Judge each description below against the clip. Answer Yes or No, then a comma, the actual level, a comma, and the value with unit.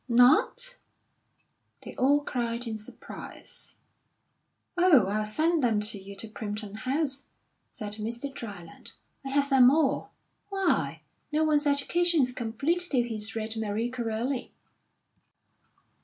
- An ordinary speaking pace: No, slow, 125 wpm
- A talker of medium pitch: No, high, 245 Hz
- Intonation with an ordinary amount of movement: Yes, average, 5.0 semitones